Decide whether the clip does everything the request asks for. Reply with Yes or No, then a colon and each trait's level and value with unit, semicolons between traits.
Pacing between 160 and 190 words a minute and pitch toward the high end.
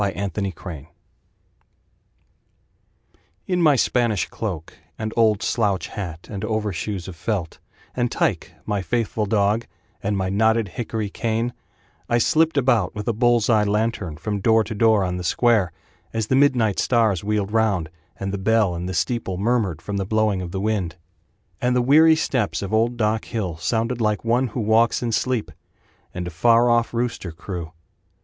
No: average, 170 wpm; low, 110 Hz